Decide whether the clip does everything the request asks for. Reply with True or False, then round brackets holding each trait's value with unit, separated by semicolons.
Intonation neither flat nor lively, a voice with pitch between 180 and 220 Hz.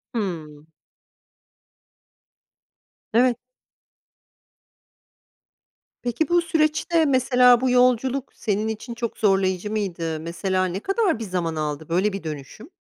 False (6.1 semitones; 215 Hz)